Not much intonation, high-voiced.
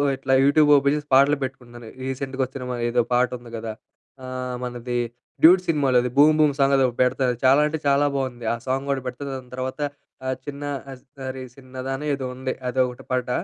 No: narrow, 1.9 semitones; low, 130 Hz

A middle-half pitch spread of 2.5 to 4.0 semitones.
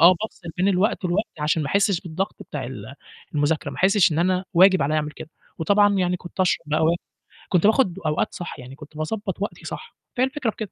No: average, 4.4 semitones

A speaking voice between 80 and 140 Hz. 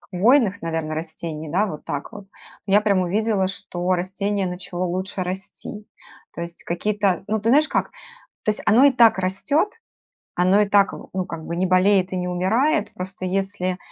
No: high, 190 Hz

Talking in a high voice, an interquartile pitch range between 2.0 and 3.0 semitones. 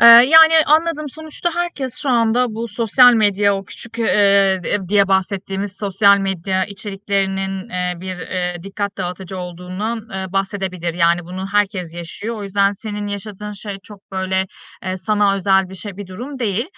Yes: high, 200 Hz; narrow, 2.6 semitones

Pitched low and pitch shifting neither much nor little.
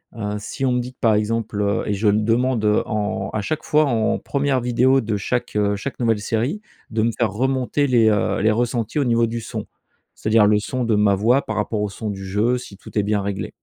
Yes: low, 110 Hz; average, 3.0 semitones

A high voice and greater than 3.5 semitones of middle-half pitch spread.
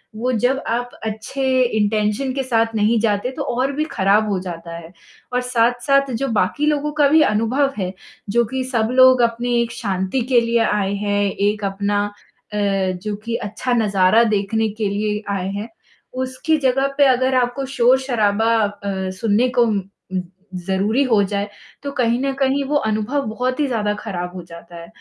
Yes: high, 225 Hz; average, 4.1 semitones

